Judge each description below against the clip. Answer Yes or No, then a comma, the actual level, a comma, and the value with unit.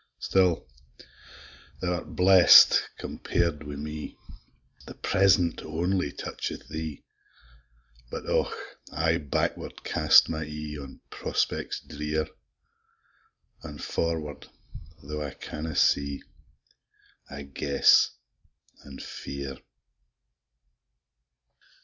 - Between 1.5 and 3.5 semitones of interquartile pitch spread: Yes, narrow, 2.6 semitones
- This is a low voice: Yes, very low, 75 Hz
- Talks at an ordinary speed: No, slow, 90 wpm